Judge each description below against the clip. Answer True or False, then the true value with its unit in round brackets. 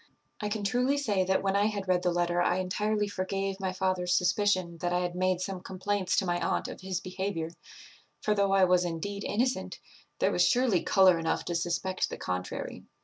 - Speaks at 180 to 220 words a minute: True (205 wpm)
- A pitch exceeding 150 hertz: True (185 Hz)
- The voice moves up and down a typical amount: False (2.2 semitones)